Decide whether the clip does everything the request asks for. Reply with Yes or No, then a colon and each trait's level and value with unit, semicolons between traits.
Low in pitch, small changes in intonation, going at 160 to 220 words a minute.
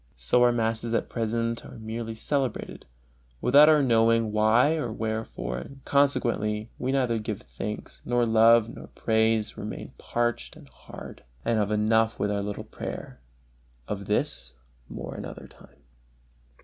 No: low, 115 Hz; narrow, 1.8 semitones; average, 145 wpm